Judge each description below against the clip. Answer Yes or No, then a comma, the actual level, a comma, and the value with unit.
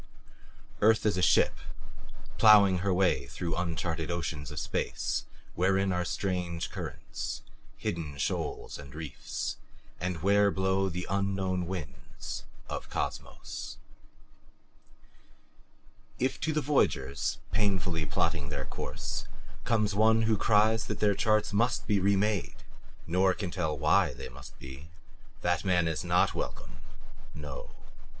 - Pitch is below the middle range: Yes, very low, 95 Hz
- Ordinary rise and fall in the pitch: Yes, average, 3.6 semitones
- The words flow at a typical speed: No, slow, 125 wpm